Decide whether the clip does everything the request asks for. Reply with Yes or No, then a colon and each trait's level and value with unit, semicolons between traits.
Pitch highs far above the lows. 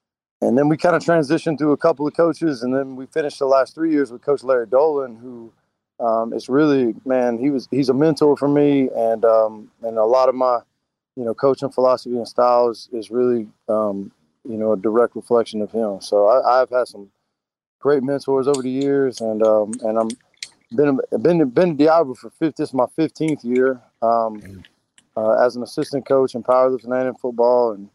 No: average, 3.9 semitones